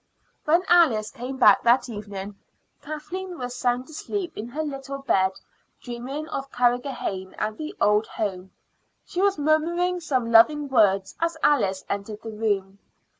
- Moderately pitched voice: No, very high, 250 Hz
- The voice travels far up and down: Yes, wide, 6.5 semitones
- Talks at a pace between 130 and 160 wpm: Yes, average, 145 wpm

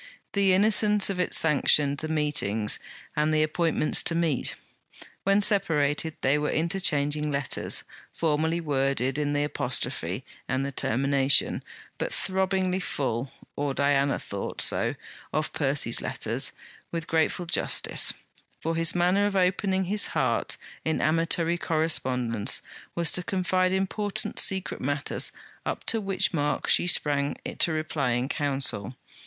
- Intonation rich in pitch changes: No, average, 4.4 semitones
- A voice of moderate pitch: Yes, medium, 155 Hz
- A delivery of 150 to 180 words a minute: No, slow, 135 wpm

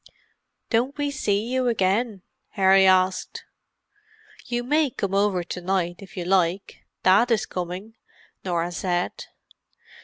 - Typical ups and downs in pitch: Yes, average, 4.2 semitones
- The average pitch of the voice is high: Yes, high, 195 Hz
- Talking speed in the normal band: No, slow, 120 wpm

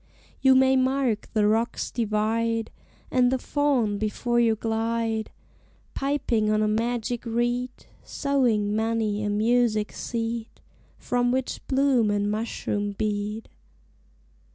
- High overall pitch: Yes, high, 230 Hz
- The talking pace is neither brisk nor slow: No, slow, 115 wpm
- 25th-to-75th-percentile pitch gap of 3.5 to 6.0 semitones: No, narrow, 2.5 semitones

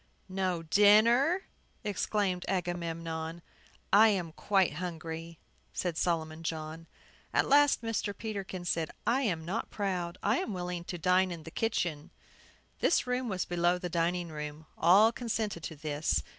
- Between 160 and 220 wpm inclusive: No, average, 145 wpm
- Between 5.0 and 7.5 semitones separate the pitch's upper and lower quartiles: No, average, 3.9 semitones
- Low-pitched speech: No, medium, 180 Hz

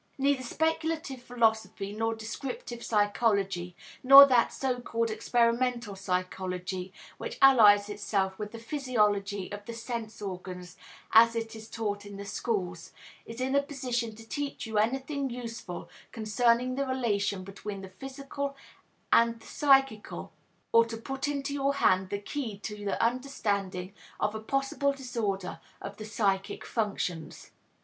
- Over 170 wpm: No, average, 140 wpm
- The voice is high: Yes, high, 225 Hz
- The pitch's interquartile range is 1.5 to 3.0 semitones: No, average, 4.2 semitones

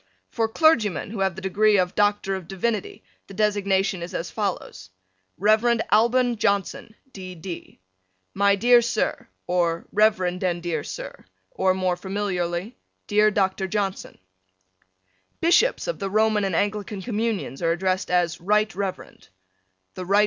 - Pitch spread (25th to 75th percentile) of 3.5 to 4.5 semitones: No, average, 2.7 semitones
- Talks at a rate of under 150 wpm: Yes, average, 140 wpm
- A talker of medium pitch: No, high, 195 Hz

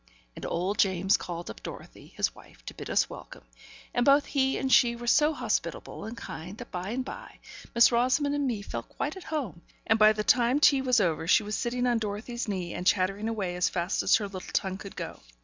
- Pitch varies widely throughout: No, average, 5.0 semitones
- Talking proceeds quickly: Yes, fast, 225 wpm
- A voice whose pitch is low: No, high, 220 Hz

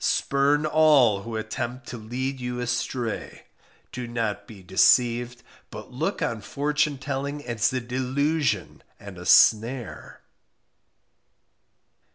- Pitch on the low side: Yes, low, 125 Hz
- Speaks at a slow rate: Yes, slow, 115 wpm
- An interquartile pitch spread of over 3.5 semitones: No, average, 3.0 semitones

